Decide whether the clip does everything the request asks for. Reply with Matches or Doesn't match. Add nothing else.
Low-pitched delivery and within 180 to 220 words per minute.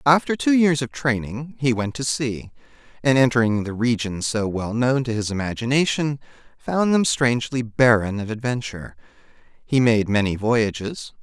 Doesn't match